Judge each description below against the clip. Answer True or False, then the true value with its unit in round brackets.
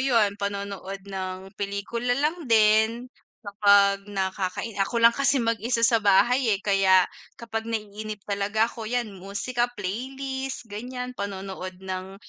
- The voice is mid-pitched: False (210 Hz)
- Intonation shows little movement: False (3.2 semitones)